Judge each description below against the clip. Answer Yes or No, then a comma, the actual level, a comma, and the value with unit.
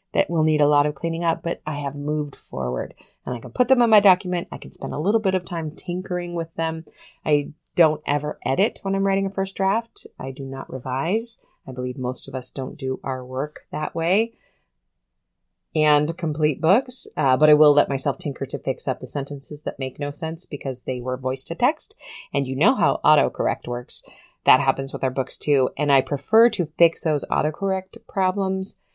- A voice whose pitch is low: No, medium, 150 Hz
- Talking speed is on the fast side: Yes, fast, 210 wpm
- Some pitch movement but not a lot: Yes, average, 4.9 semitones